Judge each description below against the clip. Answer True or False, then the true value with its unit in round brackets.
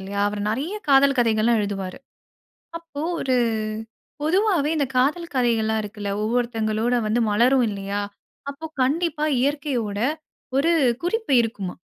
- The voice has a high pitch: True (245 Hz)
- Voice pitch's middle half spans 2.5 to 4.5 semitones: False (5.2 semitones)